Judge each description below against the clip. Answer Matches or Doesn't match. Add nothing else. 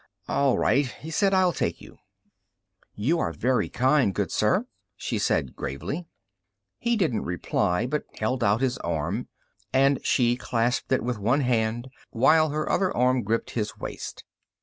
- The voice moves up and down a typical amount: Matches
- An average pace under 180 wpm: Matches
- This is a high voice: Doesn't match